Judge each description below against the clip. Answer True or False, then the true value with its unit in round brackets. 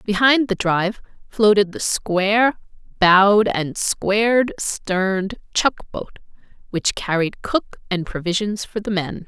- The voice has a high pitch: True (200 Hz)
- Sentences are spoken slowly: True (130 wpm)